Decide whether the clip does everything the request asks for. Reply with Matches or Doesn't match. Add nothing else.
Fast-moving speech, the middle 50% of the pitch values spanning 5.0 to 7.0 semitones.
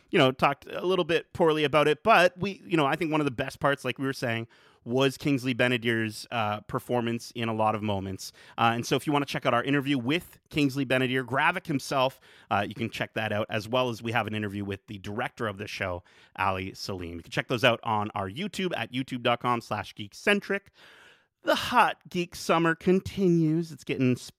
Matches